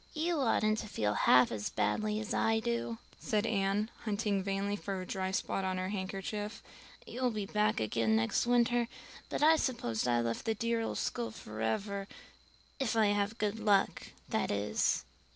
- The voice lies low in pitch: No, high, 205 Hz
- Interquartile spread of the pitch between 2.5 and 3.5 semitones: Yes, average, 3.2 semitones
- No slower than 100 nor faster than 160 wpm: No, average, 170 wpm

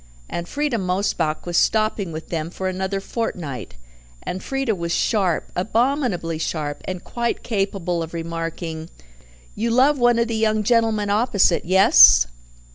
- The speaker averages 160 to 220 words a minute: No, average, 140 wpm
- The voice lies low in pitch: No, high, 190 Hz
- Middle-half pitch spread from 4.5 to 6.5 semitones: Yes, average, 5.2 semitones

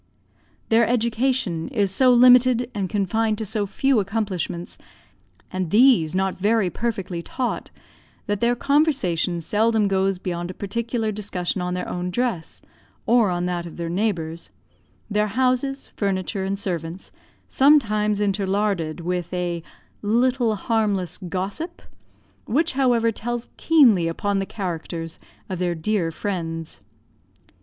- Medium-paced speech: No, slow, 125 wpm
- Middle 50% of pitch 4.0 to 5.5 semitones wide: Yes, average, 4.6 semitones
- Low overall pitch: No, high, 205 Hz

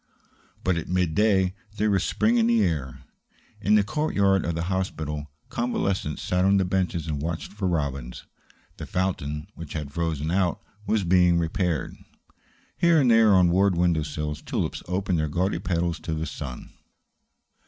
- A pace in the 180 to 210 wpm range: No, average, 165 wpm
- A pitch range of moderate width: Yes, average, 3.7 semitones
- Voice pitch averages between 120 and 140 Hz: No, very low, 90 Hz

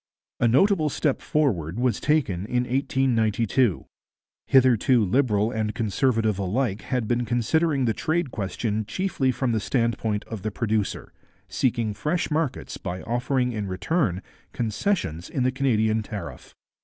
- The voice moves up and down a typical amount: Yes, average, 4.0 semitones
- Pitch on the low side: Yes, low, 120 Hz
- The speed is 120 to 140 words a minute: Yes, slow, 135 wpm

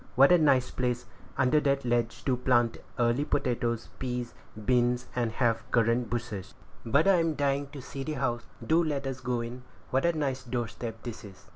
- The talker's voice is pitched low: Yes, low, 125 Hz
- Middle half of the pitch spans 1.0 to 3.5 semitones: Yes, narrow, 2.6 semitones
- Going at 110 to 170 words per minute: No, average, 185 wpm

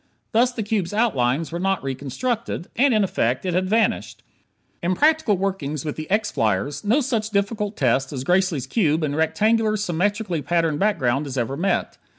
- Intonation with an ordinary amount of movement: No, wide, 6.6 semitones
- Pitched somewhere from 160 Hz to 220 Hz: Yes, medium, 185 Hz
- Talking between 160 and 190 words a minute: Yes, average, 170 wpm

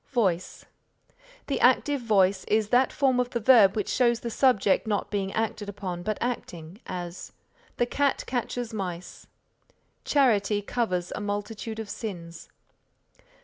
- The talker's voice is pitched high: Yes, high, 210 Hz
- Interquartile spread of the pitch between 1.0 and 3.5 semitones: No, average, 4.0 semitones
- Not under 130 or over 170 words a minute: Yes, average, 140 wpm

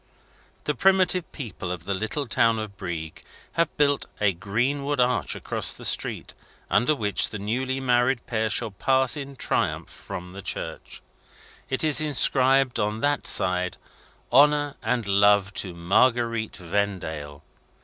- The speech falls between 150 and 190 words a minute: No, average, 140 wpm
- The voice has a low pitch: Yes, low, 115 Hz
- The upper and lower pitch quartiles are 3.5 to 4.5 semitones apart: No, wide, 5.4 semitones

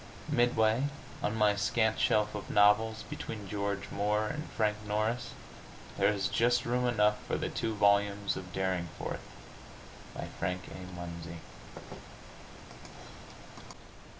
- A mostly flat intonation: Yes, narrow, 1.9 semitones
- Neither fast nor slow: No, slow, 120 wpm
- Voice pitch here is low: Yes, low, 105 Hz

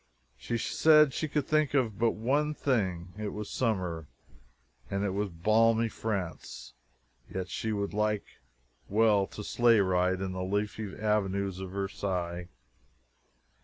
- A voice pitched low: Yes, low, 105 Hz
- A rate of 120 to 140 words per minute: Yes, slow, 135 wpm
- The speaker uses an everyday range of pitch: Yes, average, 3.3 semitones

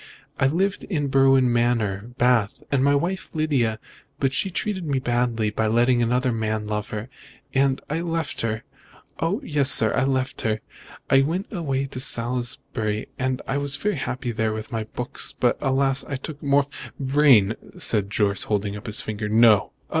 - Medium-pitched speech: No, low, 125 Hz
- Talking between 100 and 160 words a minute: No, average, 175 wpm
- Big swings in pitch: No, average, 4.1 semitones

